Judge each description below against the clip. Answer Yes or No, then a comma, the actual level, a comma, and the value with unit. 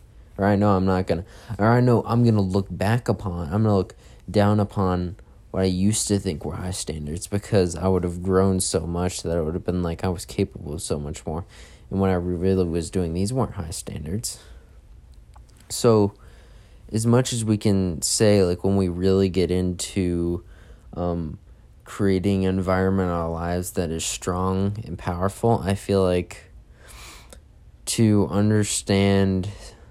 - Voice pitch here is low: Yes, very low, 95 Hz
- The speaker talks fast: No, average, 175 wpm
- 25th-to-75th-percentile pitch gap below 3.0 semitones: Yes, narrow, 2.6 semitones